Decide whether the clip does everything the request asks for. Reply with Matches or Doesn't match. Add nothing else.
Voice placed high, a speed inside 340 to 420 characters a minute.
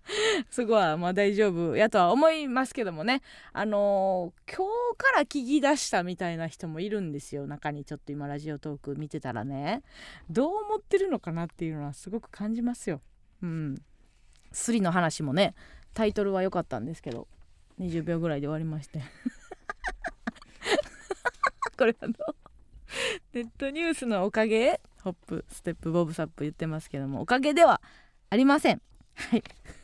Doesn't match